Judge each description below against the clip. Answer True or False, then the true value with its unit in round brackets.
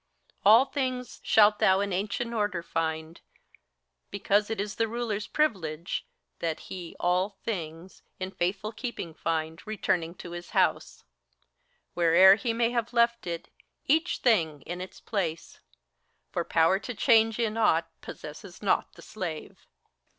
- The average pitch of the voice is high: True (195 Hz)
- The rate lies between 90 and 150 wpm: True (145 wpm)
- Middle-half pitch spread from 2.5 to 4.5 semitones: False (5.0 semitones)